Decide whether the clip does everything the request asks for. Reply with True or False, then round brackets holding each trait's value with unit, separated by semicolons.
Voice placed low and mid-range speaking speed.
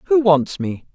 False (185 Hz; 190 wpm)